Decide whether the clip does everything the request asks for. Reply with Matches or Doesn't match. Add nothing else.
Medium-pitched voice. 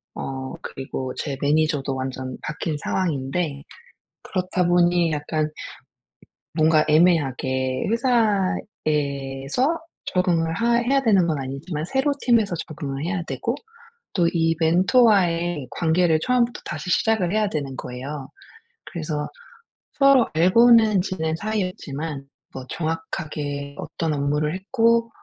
Matches